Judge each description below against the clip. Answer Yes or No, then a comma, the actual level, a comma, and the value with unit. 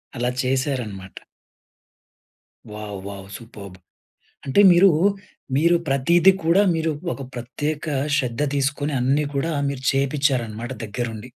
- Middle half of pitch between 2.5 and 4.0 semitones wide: No, average, 4.4 semitones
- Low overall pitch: Yes, low, 130 Hz